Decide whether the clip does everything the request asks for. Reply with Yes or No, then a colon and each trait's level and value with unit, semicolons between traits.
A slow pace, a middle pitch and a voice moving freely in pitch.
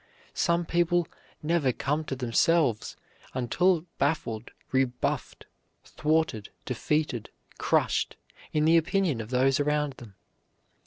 No: slow, 105 wpm; medium, 150 Hz; average, 4.7 semitones